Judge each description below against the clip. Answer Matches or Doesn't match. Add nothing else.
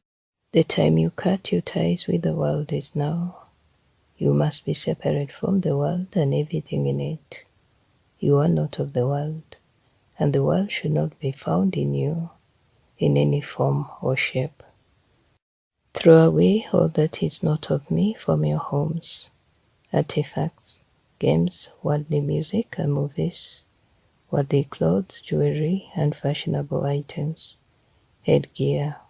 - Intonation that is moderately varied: Doesn't match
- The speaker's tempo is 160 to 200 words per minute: Doesn't match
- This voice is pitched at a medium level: Matches